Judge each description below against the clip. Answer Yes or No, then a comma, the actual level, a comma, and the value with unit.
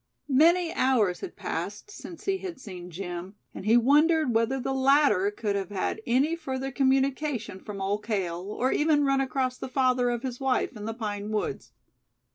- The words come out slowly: No, average, 180 wpm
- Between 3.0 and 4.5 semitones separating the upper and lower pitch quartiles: No, average, 4.9 semitones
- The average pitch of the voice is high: Yes, very high, 250 Hz